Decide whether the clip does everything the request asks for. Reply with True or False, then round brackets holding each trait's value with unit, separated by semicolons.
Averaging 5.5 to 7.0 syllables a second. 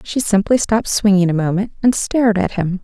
True (5.7 syllables/s)